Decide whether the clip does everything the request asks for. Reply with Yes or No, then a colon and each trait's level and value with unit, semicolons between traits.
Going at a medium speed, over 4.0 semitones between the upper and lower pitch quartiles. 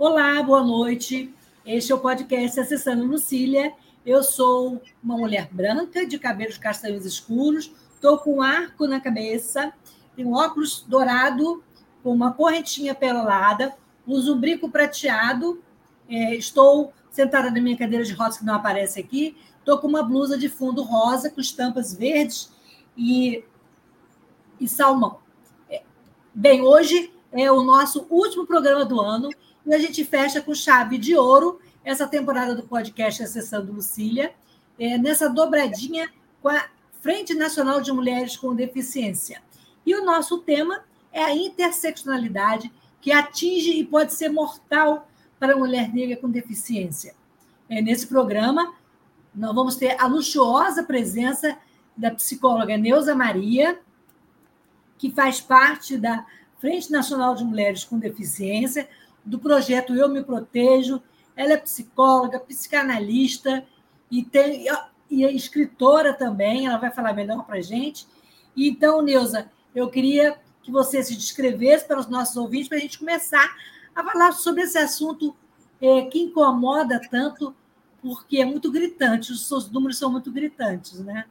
No: average, 140 wpm; average, 3.4 semitones